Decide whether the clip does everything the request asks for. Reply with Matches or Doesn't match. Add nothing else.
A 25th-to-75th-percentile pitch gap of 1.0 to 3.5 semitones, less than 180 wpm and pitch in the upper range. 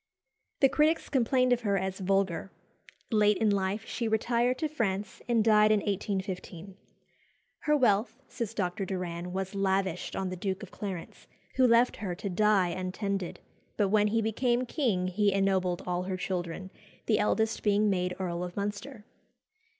Matches